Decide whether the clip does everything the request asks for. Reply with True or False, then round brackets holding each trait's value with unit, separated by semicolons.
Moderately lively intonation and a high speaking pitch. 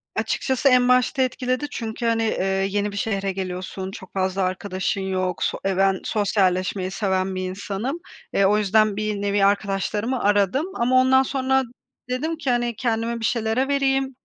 True (4.6 semitones; 210 Hz)